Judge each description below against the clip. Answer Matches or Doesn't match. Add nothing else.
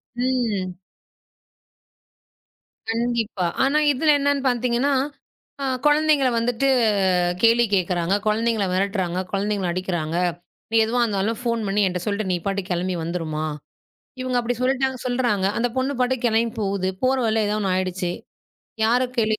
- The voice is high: Matches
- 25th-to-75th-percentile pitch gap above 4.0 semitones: Matches